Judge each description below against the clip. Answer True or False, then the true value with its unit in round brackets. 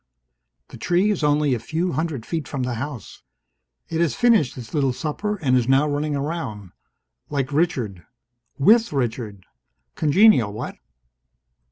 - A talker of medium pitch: True (145 Hz)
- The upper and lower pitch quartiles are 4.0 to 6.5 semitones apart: True (5.1 semitones)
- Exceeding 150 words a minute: False (145 wpm)